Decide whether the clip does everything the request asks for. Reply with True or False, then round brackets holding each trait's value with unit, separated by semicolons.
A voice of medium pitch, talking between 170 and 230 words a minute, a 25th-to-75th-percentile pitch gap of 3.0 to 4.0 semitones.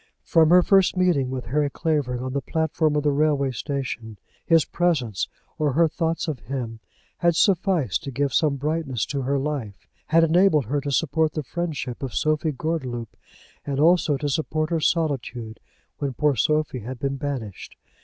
True (145 Hz; 175 wpm; 3.6 semitones)